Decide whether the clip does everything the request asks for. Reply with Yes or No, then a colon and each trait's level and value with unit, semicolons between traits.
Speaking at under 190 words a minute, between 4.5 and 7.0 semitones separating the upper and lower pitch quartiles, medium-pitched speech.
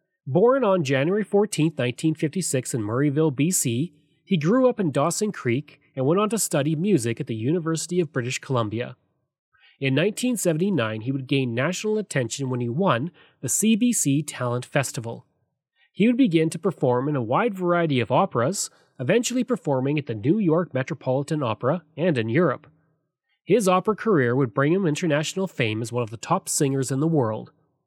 Yes: average, 170 wpm; wide, 5.4 semitones; medium, 155 Hz